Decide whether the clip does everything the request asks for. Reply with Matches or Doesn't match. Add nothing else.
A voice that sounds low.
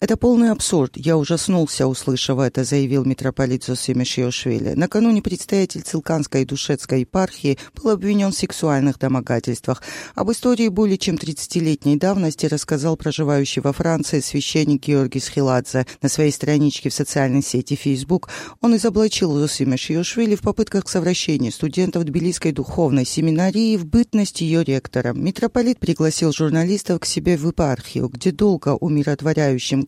Doesn't match